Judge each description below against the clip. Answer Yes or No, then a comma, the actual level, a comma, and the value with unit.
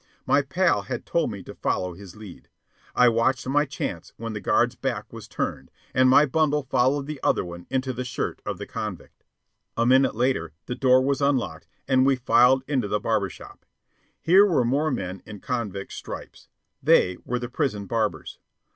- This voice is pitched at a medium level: No, low, 125 Hz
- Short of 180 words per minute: No, average, 185 wpm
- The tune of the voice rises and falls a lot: No, average, 4.3 semitones